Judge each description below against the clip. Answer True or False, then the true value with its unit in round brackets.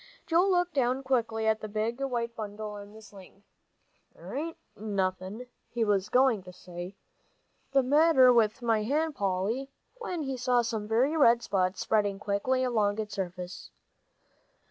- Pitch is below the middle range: False (225 Hz)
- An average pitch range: True (4.3 semitones)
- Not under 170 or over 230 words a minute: False (160 wpm)